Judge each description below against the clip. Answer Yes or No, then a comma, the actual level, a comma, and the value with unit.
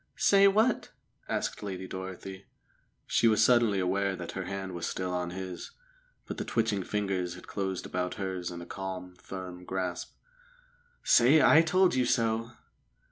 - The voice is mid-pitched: No, very low, 95 Hz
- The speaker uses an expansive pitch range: No, average, 3.9 semitones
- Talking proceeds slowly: No, average, 155 wpm